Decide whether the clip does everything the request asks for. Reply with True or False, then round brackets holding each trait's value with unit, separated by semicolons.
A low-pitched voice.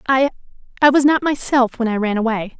False (250 Hz)